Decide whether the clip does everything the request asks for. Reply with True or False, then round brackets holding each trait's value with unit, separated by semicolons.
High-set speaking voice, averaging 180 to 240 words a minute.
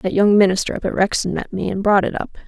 False (195 Hz; 290 wpm)